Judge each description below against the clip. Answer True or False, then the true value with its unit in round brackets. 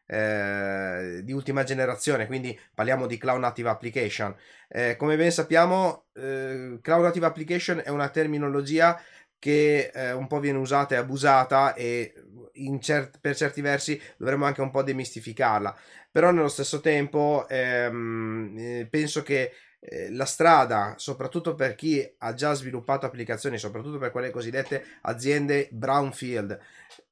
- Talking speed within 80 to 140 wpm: True (135 wpm)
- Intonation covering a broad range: False (3.2 semitones)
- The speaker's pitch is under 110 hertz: False (135 Hz)